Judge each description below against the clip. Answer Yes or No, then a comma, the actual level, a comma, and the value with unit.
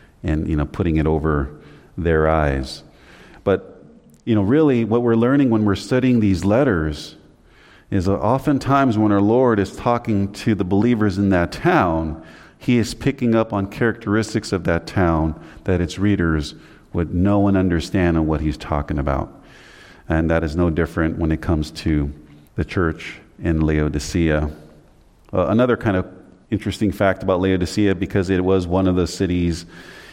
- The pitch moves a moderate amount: Yes, average, 4.6 semitones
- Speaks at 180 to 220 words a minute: No, average, 165 wpm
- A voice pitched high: No, very low, 90 Hz